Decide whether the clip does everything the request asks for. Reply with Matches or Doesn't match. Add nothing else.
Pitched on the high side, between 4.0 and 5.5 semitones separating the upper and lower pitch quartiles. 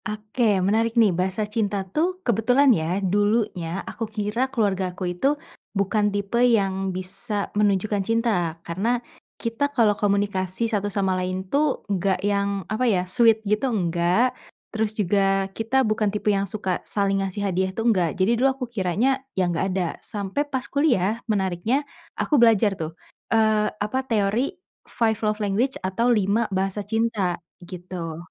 Doesn't match